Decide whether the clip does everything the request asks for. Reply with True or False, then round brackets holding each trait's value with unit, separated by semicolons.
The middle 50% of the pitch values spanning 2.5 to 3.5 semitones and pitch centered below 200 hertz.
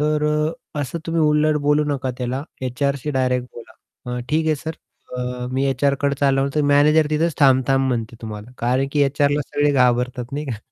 True (2.9 semitones; 140 Hz)